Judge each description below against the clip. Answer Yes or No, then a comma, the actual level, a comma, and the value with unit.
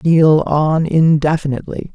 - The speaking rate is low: Yes, slow, 90 wpm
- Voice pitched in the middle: Yes, medium, 155 Hz